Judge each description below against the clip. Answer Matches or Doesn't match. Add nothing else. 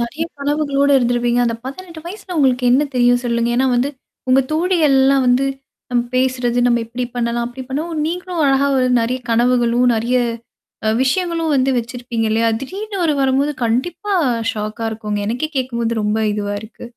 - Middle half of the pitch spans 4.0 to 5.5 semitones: Doesn't match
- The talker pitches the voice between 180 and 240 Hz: Doesn't match